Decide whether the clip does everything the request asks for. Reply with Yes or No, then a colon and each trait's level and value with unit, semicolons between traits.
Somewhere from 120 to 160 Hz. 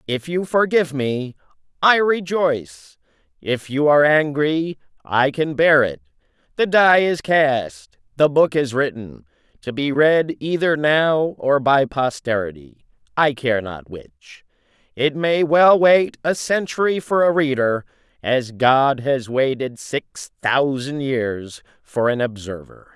Yes: medium, 140 Hz